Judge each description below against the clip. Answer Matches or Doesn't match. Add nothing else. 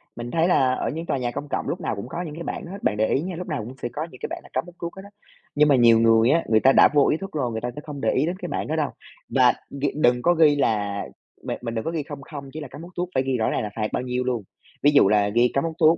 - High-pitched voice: Doesn't match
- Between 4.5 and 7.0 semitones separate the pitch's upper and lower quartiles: Matches